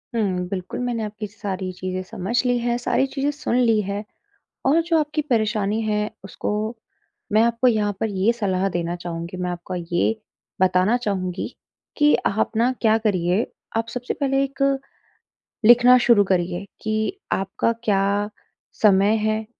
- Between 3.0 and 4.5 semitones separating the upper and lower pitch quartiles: Yes, average, 4.1 semitones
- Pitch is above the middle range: Yes, high, 210 Hz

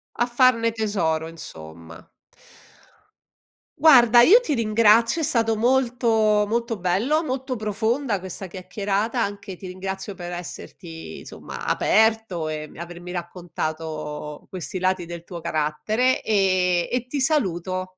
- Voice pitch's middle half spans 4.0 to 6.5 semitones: Yes, average, 5.1 semitones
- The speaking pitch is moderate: No, high, 200 Hz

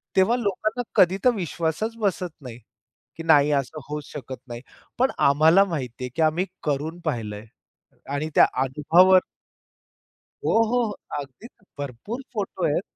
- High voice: No, medium, 160 Hz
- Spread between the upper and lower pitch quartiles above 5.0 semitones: Yes, wide, 5.5 semitones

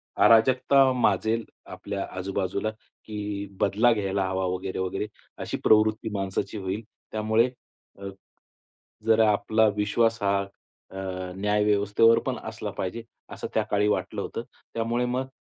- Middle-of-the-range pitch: No, low, 105 Hz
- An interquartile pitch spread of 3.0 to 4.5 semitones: No, narrow, 2.5 semitones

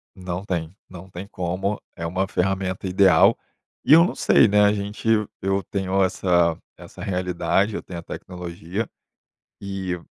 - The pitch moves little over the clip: Yes, narrow, 1.8 semitones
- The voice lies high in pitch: No, very low, 95 Hz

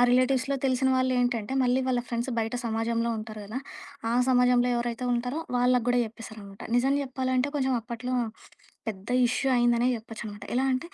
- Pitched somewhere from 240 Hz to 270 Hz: Yes, high, 245 Hz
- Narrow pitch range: Yes, narrow, 2.0 semitones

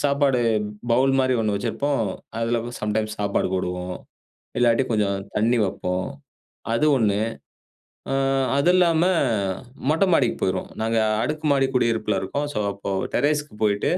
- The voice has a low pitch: Yes, low, 115 Hz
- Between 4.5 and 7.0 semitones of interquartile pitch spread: Yes, wide, 5.4 semitones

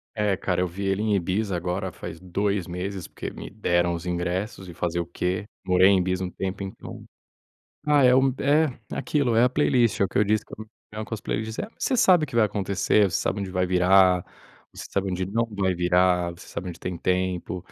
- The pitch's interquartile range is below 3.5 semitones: Yes, average, 2.9 semitones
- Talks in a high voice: No, very low, 95 Hz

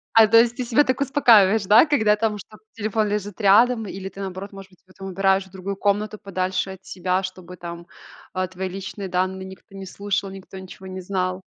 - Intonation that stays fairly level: Yes, narrow, 2.2 semitones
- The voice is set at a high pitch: Yes, high, 195 Hz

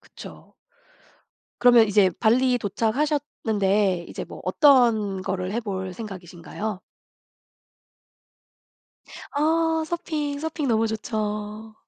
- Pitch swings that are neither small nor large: No, wide, 5.8 semitones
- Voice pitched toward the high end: Yes, high, 220 Hz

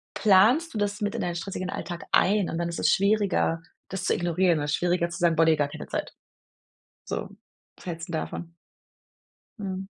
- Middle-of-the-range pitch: Yes, medium, 175 Hz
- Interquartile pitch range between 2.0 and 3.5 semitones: Yes, average, 2.9 semitones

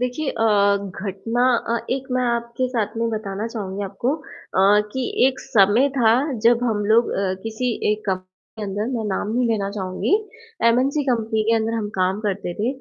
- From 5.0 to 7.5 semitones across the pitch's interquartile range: No, average, 3.3 semitones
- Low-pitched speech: No, high, 225 Hz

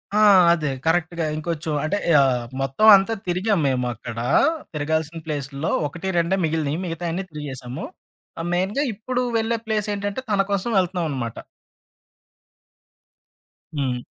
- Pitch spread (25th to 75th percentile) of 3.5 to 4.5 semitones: No, average, 5.2 semitones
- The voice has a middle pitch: Yes, medium, 165 Hz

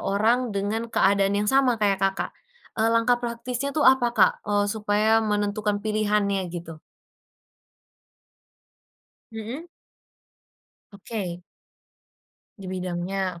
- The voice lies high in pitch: Yes, high, 210 Hz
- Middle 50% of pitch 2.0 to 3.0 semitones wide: Yes, average, 2.7 semitones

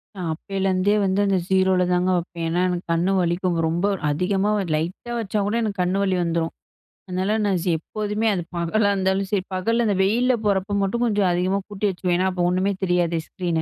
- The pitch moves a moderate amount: No, narrow, 2.2 semitones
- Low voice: No, high, 190 Hz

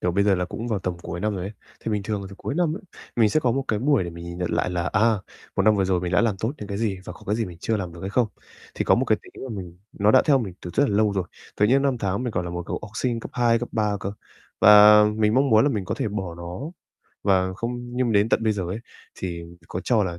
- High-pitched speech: No, low, 105 Hz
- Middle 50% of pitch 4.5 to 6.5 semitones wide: No, average, 3.8 semitones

